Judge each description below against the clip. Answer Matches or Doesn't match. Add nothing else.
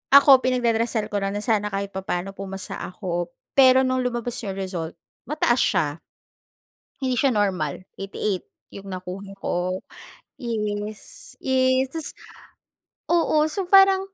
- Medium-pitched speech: Doesn't match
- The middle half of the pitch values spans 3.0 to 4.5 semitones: Doesn't match